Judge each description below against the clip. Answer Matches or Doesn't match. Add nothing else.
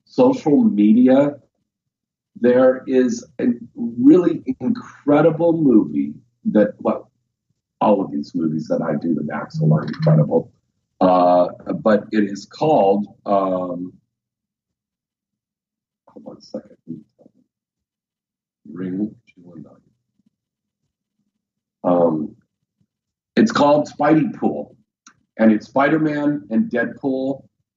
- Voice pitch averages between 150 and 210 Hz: Doesn't match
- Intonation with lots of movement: Matches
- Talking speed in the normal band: Doesn't match